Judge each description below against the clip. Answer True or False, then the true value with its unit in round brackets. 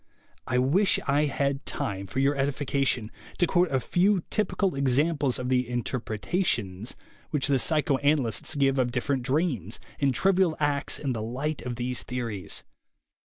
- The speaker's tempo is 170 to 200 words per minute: False (150 wpm)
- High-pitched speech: False (135 Hz)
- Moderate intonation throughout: True (3.5 semitones)